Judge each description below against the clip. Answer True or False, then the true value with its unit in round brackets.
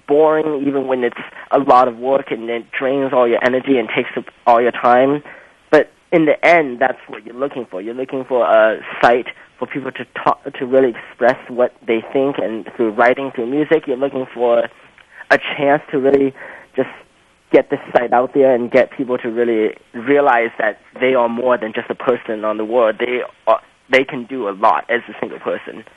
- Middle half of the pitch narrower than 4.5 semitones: True (2.5 semitones)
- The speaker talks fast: True (210 wpm)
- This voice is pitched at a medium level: False (125 Hz)